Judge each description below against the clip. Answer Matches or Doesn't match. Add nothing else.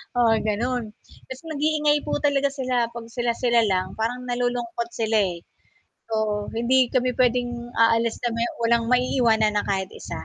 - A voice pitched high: Matches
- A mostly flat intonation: Matches